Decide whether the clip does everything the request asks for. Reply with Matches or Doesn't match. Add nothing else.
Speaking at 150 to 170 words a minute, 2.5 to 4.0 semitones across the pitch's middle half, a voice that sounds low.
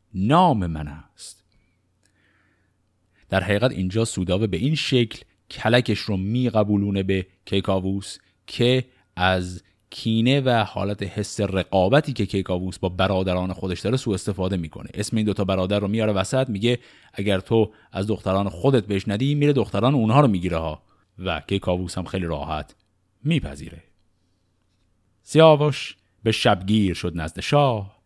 Doesn't match